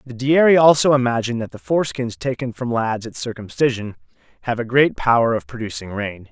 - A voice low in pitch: Yes, low, 120 Hz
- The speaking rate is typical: Yes, average, 180 wpm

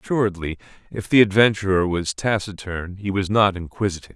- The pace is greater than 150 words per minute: No, average, 145 wpm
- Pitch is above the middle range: No, very low, 95 Hz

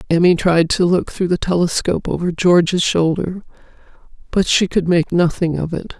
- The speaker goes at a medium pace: Yes, average, 170 wpm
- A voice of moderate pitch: Yes, medium, 175 Hz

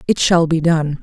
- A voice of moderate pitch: Yes, medium, 160 Hz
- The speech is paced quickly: Yes, fast, 235 wpm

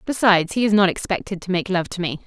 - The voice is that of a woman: Yes, female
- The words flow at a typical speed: No, fast, 265 wpm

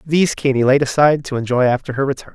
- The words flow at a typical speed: No, fast, 230 wpm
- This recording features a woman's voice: No, male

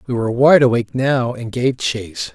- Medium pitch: No, low, 125 Hz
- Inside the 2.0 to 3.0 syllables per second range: No, 5.5 syllables/s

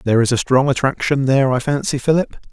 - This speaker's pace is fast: Yes, fast, 215 wpm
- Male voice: Yes, male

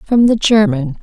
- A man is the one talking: No, female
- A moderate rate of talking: Yes, average, 175 wpm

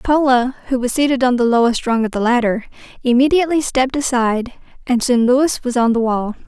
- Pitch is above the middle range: Yes, very high, 250 Hz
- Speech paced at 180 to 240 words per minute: Yes, average, 195 wpm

